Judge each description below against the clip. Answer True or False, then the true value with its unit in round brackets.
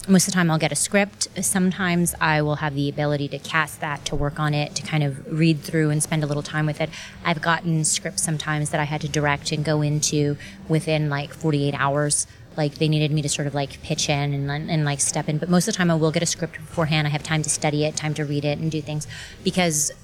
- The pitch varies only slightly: True (1.6 semitones)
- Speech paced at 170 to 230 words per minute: False (265 wpm)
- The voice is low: False (155 Hz)